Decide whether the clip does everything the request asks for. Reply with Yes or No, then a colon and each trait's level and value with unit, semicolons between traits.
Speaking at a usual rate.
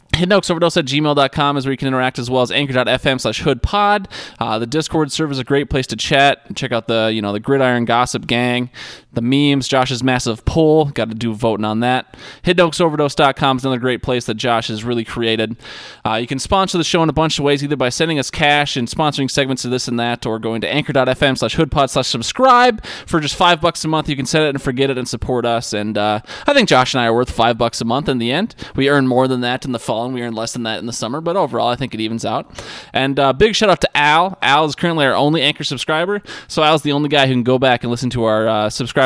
No: fast, 265 wpm